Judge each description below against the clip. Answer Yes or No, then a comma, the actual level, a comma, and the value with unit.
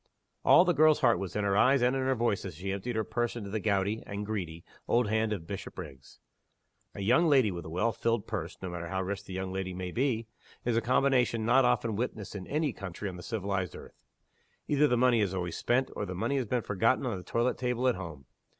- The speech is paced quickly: Yes, fast, 240 wpm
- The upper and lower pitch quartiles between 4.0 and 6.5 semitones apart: Yes, average, 4.6 semitones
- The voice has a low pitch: Yes, low, 110 Hz